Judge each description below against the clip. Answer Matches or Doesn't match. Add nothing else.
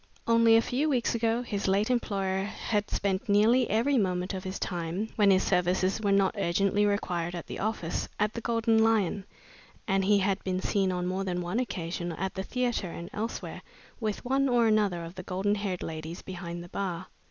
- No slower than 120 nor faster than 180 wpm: Doesn't match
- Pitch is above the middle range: Matches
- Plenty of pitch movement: Doesn't match